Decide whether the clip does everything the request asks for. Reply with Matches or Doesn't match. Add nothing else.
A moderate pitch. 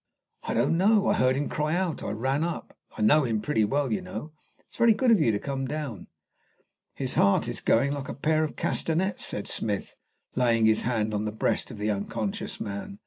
Doesn't match